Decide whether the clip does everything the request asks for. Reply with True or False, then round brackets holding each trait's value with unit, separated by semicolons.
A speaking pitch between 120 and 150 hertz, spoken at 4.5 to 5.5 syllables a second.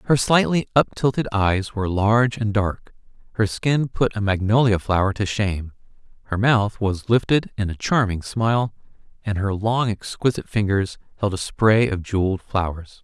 False (105 Hz; 4.9 syllables/s)